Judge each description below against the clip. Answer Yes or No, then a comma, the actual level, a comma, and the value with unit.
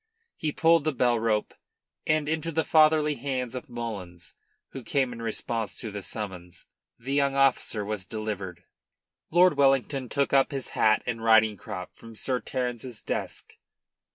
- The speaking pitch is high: No, low, 120 Hz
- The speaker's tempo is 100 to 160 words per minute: Yes, average, 155 wpm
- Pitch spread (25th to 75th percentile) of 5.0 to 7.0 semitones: No, average, 4.5 semitones